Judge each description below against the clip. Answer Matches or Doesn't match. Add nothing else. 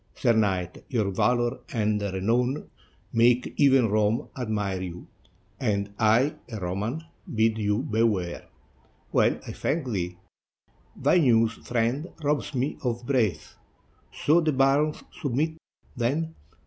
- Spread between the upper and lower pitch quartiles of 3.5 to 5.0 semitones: Matches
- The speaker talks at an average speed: Doesn't match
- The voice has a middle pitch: Doesn't match